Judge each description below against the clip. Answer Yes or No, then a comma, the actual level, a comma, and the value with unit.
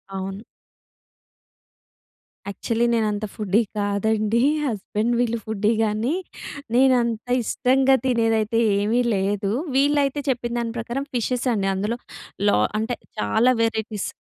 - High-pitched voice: Yes, high, 225 Hz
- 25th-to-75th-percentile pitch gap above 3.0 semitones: No, narrow, 2.6 semitones